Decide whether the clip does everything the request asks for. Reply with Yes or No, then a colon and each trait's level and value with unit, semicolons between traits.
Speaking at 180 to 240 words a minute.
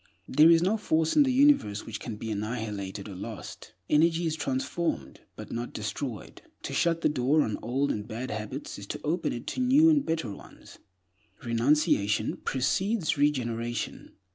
No: average, 165 wpm